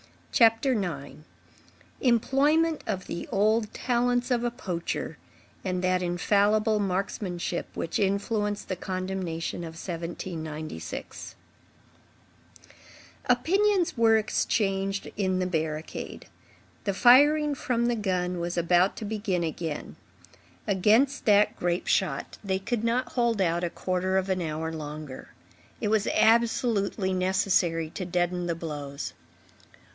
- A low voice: No, high, 190 Hz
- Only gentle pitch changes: No, average, 4.6 semitones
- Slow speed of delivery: Yes, slow, 115 wpm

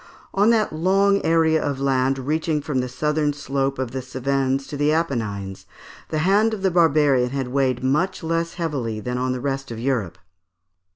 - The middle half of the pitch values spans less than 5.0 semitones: Yes, average, 3.8 semitones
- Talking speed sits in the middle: Yes, average, 180 wpm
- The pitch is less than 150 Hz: Yes, medium, 140 Hz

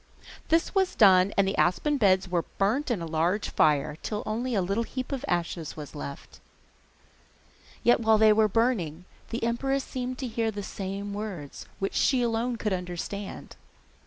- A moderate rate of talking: Yes, average, 170 wpm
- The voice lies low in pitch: No, high, 210 Hz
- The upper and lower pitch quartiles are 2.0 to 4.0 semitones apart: No, average, 4.6 semitones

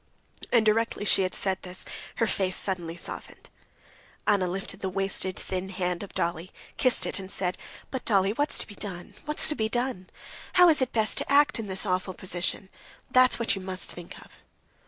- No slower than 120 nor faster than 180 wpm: No, average, 190 wpm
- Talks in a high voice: Yes, high, 195 Hz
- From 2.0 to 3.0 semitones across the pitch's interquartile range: No, average, 3.6 semitones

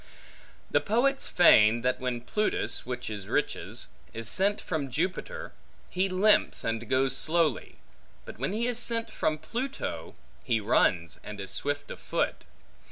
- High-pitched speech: No, medium, 155 Hz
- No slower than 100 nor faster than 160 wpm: Yes, average, 150 wpm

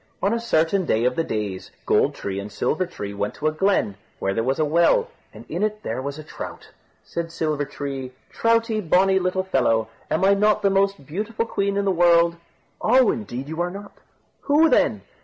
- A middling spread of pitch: No, wide, 6.6 semitones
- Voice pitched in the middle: Yes, medium, 170 Hz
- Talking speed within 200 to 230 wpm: Yes, fast, 205 wpm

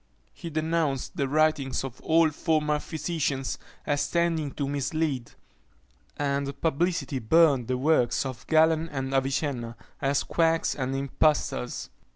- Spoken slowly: Yes, slow, 125 wpm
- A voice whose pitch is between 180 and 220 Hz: No, medium, 145 Hz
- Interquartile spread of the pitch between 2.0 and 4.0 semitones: Yes, average, 3.1 semitones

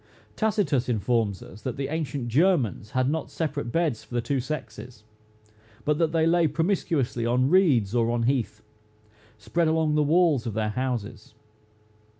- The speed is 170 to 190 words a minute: No, average, 155 wpm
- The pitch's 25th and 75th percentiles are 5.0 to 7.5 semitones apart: Yes, wide, 5.4 semitones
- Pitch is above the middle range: No, low, 130 Hz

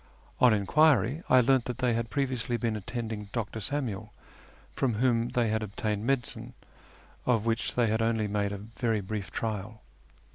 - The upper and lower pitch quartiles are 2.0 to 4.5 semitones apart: Yes, narrow, 2.5 semitones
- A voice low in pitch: Yes, low, 115 Hz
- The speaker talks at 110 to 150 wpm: No, average, 160 wpm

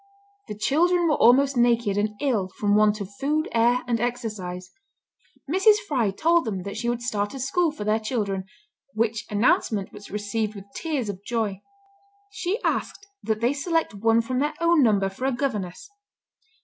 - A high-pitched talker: Yes, high, 230 Hz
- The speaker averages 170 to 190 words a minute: Yes, average, 175 wpm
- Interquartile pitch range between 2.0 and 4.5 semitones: No, average, 5.1 semitones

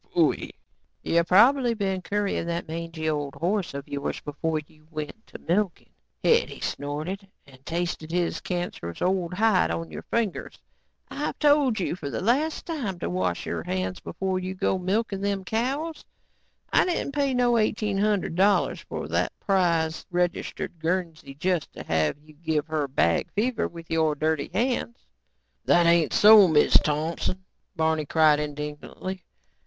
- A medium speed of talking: Yes, average, 155 wpm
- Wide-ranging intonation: No, average, 4.8 semitones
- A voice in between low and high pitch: Yes, medium, 175 Hz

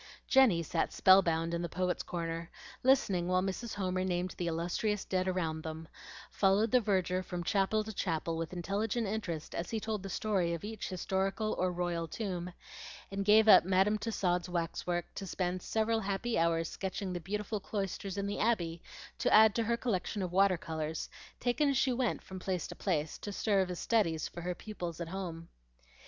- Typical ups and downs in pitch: Yes, average, 3.4 semitones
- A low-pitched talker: No, medium, 185 Hz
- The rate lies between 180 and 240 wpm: Yes, average, 190 wpm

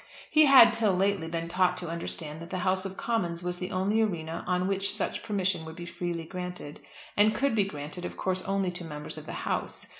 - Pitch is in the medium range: Yes, medium, 180 Hz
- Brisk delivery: Yes, fast, 220 wpm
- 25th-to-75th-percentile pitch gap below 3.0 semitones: Yes, narrow, 2.6 semitones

